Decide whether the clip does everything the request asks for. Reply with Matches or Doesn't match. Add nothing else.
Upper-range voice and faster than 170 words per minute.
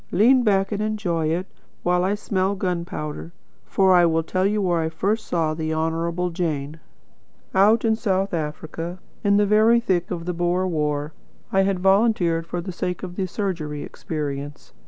Doesn't match